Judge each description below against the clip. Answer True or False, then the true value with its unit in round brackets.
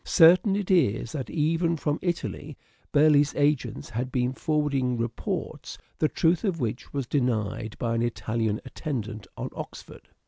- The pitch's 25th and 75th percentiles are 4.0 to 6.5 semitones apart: True (5.1 semitones)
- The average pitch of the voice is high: False (140 Hz)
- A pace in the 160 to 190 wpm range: False (145 wpm)